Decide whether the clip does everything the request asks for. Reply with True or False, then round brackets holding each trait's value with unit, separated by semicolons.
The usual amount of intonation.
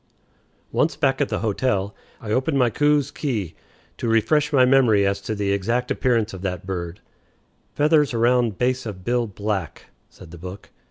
True (4.8 semitones)